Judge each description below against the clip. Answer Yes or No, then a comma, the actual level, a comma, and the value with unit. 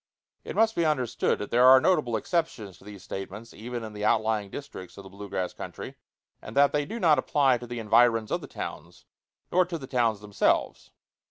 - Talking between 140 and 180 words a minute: No, fast, 205 wpm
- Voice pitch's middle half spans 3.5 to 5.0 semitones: No, wide, 5.4 semitones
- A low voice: Yes, low, 120 Hz